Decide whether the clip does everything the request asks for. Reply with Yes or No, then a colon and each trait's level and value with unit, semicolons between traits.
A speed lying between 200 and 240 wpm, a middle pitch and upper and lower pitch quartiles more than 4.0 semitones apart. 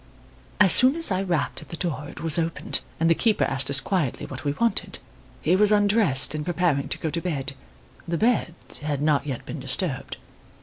Yes: fast, 205 wpm; medium, 165 Hz; average, 5.2 semitones